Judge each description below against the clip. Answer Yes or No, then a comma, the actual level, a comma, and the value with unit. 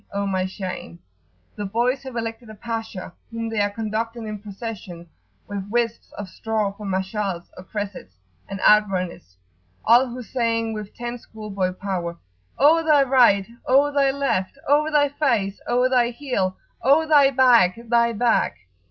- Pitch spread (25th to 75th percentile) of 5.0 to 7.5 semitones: No, average, 4.0 semitones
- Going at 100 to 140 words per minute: No, average, 150 wpm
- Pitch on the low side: No, high, 225 Hz